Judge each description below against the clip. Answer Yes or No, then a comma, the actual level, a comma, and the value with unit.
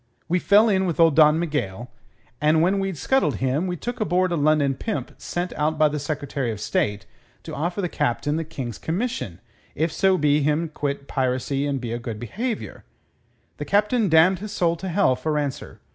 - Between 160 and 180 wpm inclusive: No, average, 195 wpm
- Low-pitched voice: No, medium, 155 Hz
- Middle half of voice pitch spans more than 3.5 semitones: Yes, average, 4.7 semitones